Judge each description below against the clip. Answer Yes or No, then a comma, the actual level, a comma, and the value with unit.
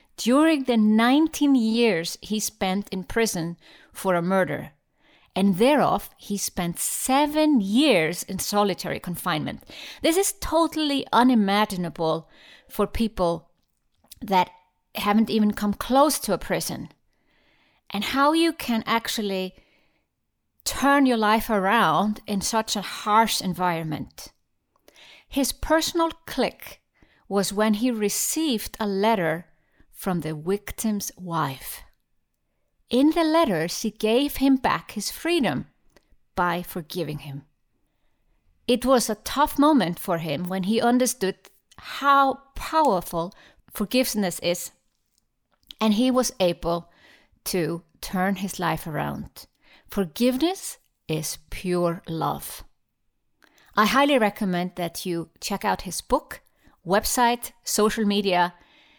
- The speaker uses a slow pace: Yes, slow, 115 wpm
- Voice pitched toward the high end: Yes, high, 210 Hz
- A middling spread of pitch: No, wide, 6.2 semitones